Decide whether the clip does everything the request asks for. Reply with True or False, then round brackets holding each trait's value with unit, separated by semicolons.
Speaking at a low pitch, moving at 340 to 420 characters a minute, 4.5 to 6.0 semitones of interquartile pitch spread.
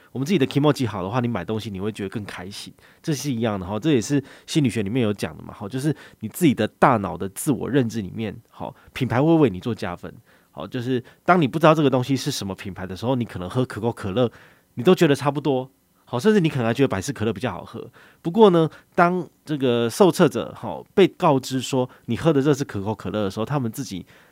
True (125 Hz; 365 characters per minute; 5.1 semitones)